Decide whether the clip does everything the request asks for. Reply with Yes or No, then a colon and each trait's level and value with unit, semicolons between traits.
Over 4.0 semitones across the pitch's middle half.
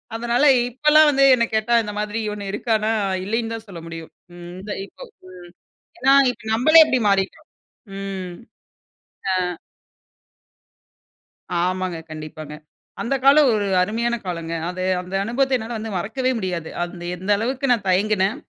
Yes: average, 4.6 semitones